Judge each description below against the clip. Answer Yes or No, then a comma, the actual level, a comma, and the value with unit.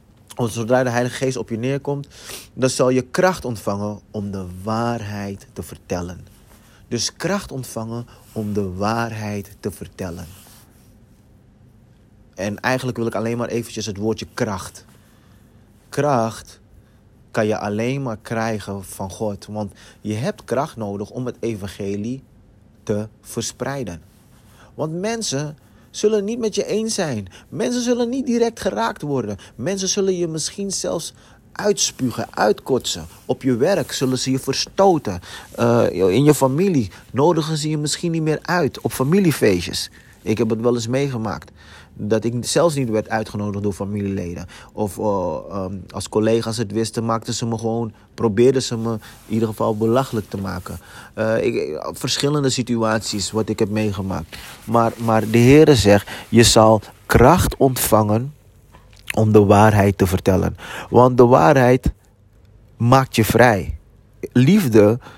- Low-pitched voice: Yes, low, 115 Hz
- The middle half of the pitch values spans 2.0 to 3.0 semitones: No, average, 3.7 semitones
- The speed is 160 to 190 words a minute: No, average, 145 wpm